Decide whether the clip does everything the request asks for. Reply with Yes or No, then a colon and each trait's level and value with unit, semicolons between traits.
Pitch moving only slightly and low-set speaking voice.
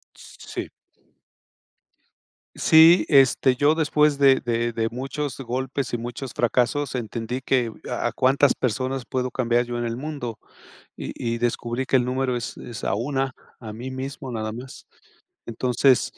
Yes: narrow, 2.2 semitones; low, 125 Hz